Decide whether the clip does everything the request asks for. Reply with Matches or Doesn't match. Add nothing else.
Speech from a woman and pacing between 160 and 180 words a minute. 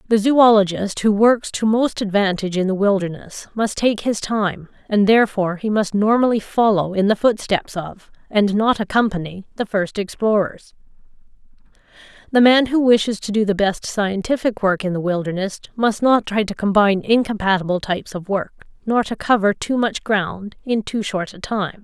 Matches